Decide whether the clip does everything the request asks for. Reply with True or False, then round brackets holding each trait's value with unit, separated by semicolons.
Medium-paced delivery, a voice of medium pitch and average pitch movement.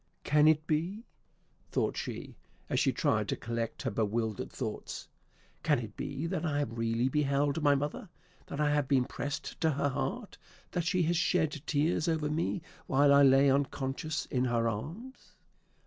True (170 wpm; 145 Hz; 3.2 semitones)